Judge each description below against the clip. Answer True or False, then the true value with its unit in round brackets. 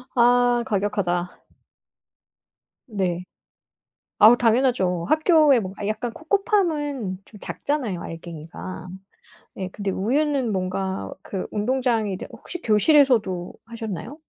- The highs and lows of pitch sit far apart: True (5.9 semitones)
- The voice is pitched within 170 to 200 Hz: False (220 Hz)